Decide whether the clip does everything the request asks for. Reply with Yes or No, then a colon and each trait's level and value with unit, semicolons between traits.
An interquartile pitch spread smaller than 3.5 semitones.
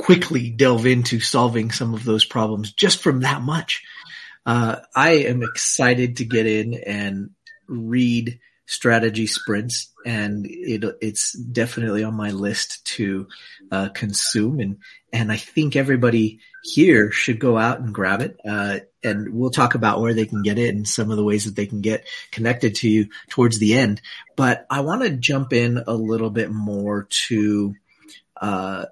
Yes: average, 2.7 semitones